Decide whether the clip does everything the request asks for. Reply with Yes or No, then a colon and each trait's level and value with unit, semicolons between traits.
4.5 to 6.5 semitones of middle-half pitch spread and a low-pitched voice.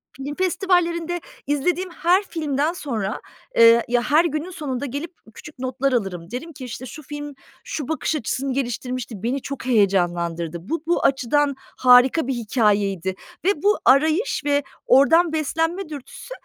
No: average, 5.2 semitones; very high, 275 Hz